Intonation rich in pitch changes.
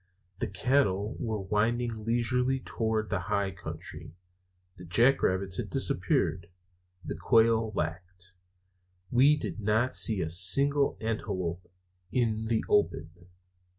No: average, 4.3 semitones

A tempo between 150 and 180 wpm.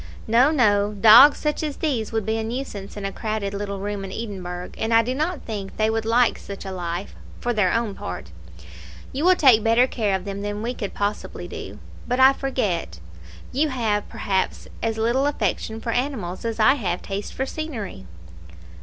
No: average, 195 wpm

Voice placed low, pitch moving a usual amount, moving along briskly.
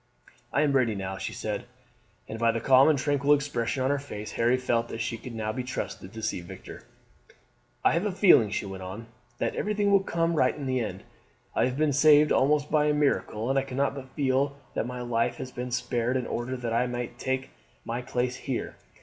Yes: low, 130 Hz; average, 3.5 semitones; fast, 220 wpm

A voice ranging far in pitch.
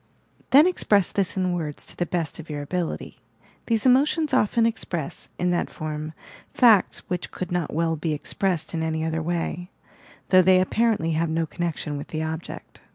No: average, 3.5 semitones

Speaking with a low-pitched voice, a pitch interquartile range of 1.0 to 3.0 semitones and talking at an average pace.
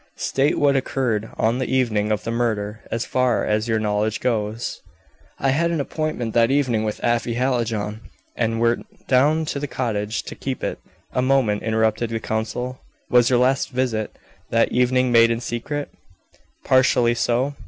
Yes: low, 120 Hz; average, 2.7 semitones; average, 165 wpm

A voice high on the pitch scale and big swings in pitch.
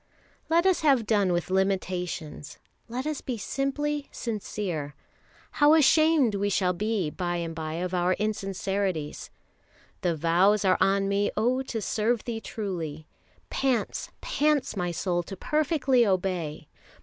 Yes: high, 200 Hz; wide, 6.0 semitones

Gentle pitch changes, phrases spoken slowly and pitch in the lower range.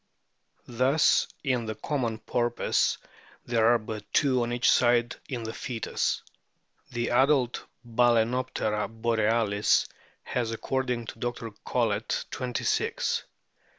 Yes: narrow, 1.8 semitones; slow, 115 wpm; low, 120 Hz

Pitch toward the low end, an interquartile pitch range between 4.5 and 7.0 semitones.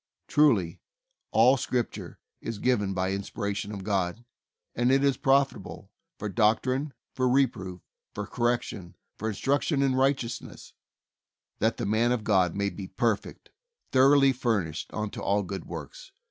Yes: low, 115 Hz; average, 4.8 semitones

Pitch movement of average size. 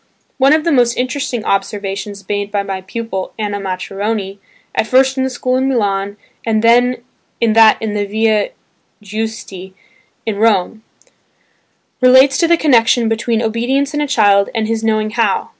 Yes: average, 3.6 semitones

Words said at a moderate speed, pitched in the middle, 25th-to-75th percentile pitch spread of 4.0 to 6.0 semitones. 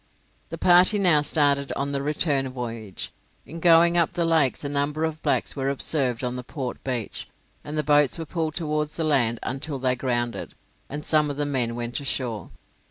No: average, 190 wpm; medium, 145 Hz; average, 3.5 semitones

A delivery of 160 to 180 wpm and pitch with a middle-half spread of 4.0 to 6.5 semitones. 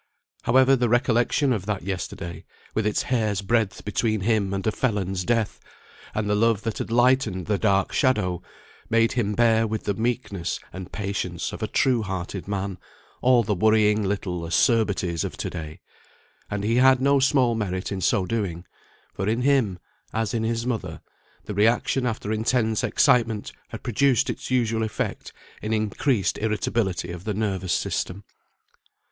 No: average, 165 wpm; average, 3.2 semitones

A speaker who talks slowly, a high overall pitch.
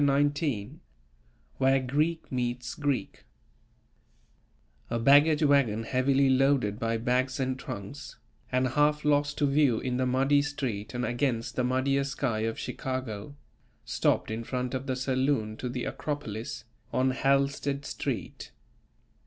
No: slow, 130 wpm; low, 130 Hz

